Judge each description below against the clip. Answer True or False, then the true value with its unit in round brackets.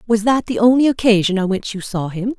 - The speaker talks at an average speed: False (250 wpm)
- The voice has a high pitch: True (220 Hz)